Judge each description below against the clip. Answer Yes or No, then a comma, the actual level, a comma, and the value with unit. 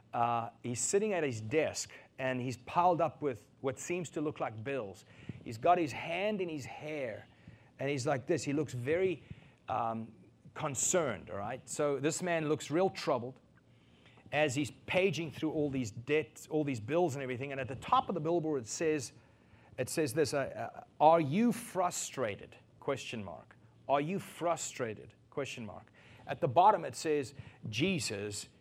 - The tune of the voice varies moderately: Yes, average, 4.7 semitones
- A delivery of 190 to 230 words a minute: No, average, 170 wpm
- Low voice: No, medium, 145 Hz